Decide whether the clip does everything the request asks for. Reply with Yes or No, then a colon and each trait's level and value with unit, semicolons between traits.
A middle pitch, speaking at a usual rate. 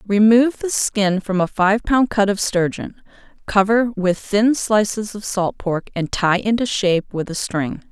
No: high, 205 Hz; average, 180 wpm